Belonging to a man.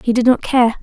No: female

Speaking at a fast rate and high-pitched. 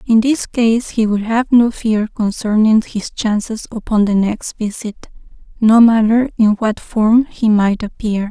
No: average, 165 wpm; high, 220 Hz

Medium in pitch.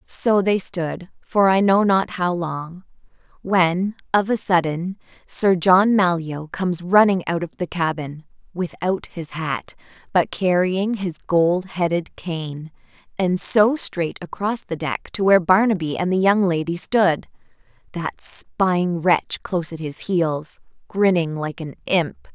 Yes: medium, 180 Hz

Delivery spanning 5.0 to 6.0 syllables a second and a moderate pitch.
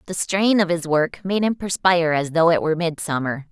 Yes: 5.5 syllables/s; medium, 170 Hz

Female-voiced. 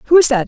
Yes: female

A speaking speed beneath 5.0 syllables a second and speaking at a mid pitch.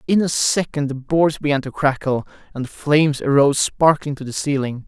No: 5.4 syllables/s; medium, 145 Hz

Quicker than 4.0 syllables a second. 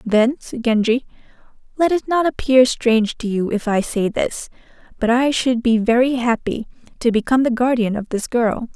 Yes: 5.0 syllables/s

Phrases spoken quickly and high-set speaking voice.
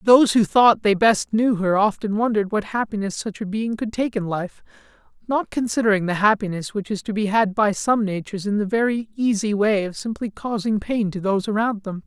Yes: fast, 215 wpm; high, 210 Hz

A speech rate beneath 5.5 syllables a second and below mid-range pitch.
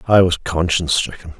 No: 5.8 syllables/s; very low, 85 Hz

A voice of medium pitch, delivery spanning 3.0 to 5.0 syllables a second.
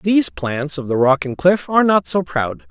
Yes: medium, 155 Hz; 4.9 syllables/s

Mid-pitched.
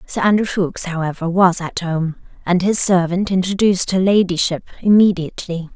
Yes: medium, 180 Hz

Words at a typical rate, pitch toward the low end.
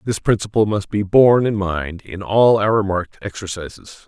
Yes: average, 175 wpm; low, 100 Hz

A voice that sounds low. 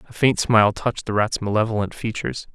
Yes: low, 110 Hz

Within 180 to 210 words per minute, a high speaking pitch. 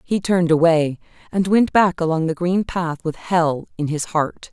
No: average, 200 wpm; medium, 170 Hz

